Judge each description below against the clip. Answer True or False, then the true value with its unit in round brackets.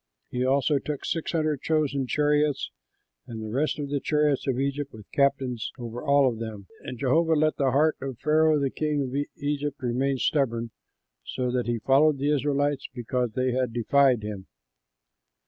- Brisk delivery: False (170 wpm)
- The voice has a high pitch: False (140 Hz)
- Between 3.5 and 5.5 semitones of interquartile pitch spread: False (3.0 semitones)